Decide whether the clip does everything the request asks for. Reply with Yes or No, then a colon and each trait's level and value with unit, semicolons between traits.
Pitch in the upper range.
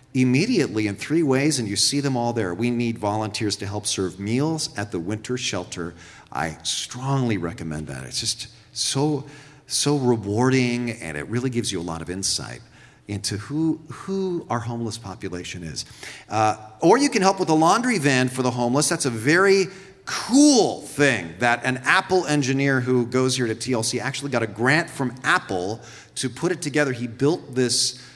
No: low, 125 Hz